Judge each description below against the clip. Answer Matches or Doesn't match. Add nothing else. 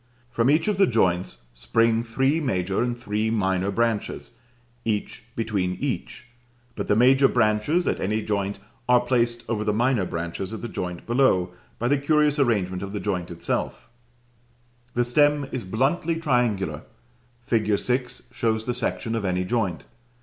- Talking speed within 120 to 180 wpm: Matches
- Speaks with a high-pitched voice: Doesn't match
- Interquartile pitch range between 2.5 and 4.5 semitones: Matches